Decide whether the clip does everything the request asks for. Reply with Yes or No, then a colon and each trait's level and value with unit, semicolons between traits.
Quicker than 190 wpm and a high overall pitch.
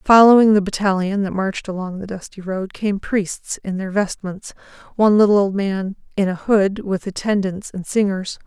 No: average, 170 wpm; high, 195 Hz